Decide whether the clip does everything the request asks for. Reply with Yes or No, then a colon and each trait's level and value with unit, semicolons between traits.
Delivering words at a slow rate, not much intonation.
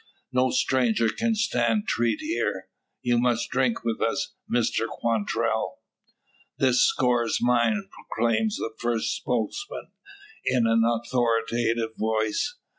Yes: slow, 115 wpm; narrow, 1.9 semitones